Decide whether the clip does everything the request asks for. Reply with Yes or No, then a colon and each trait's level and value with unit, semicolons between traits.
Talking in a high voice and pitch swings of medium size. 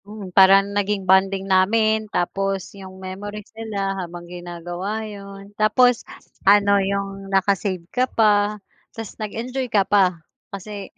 No: high, 200 Hz; narrow, 1.8 semitones